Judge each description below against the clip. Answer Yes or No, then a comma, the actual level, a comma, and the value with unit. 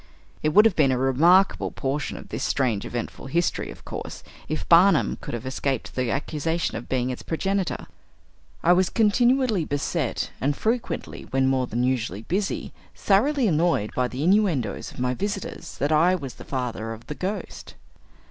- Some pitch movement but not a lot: No, wide, 6.8 semitones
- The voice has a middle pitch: Yes, medium, 150 Hz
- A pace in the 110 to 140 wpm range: No, average, 170 wpm